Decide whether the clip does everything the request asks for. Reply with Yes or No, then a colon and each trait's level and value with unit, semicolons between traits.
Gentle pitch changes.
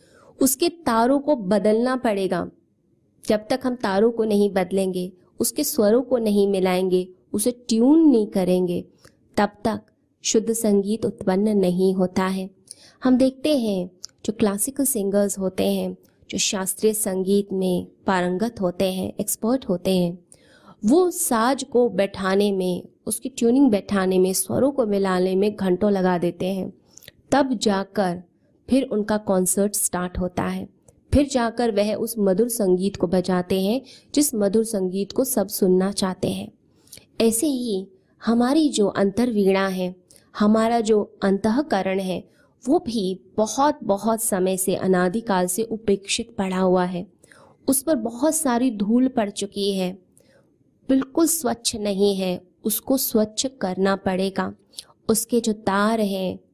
No: average, 3.8 semitones